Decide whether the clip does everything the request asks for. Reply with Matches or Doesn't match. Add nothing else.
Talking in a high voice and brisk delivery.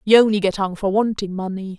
Matches